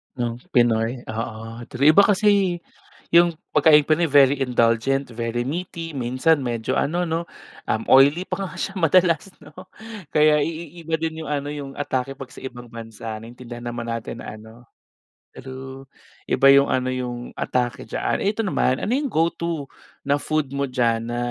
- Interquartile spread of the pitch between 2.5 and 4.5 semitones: No, average, 5.1 semitones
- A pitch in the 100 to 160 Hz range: Yes, low, 135 Hz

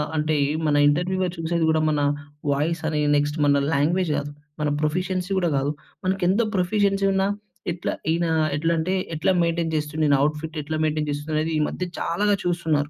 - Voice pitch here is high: No, medium, 160 Hz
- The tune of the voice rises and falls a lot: No, average, 3.0 semitones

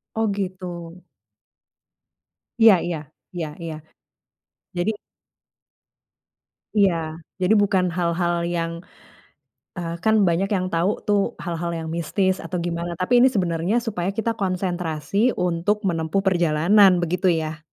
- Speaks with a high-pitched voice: No, medium, 180 Hz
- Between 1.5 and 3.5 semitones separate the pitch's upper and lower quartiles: Yes, average, 2.8 semitones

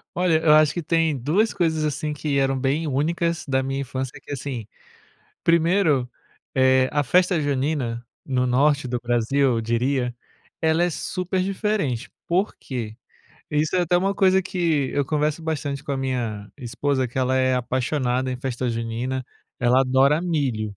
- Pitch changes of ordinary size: Yes, average, 3.9 semitones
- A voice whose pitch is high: No, medium, 140 Hz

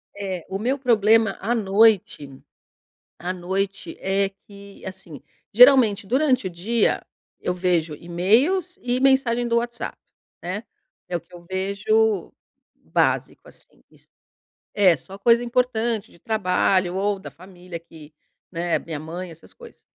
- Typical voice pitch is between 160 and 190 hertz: No, high, 200 Hz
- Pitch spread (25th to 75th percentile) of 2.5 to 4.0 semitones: No, average, 4.5 semitones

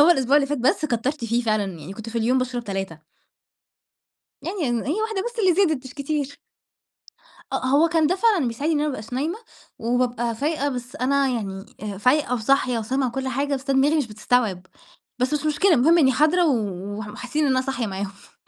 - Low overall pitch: No, very high, 260 Hz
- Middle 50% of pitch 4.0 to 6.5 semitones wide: Yes, average, 4.6 semitones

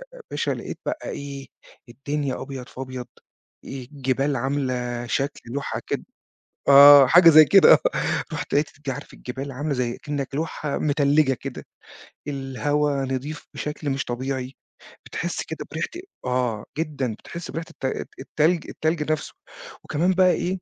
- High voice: No, medium, 140 Hz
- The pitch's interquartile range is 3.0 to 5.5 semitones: No, narrow, 2.5 semitones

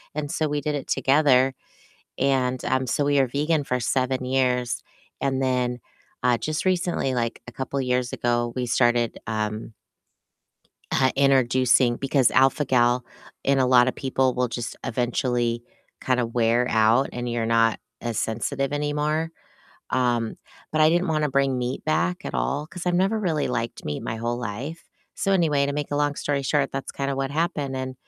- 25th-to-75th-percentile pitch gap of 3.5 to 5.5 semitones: No, average, 3.0 semitones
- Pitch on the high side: No, low, 130 Hz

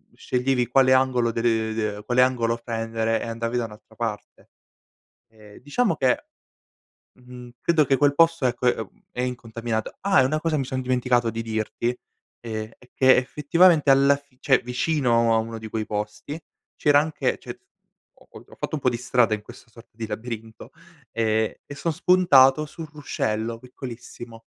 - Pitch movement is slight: No, average, 3.1 semitones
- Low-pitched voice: Yes, low, 125 Hz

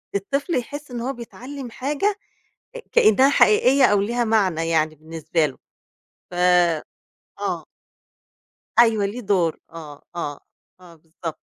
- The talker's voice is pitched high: Yes, high, 200 Hz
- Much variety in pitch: Yes, wide, 7.3 semitones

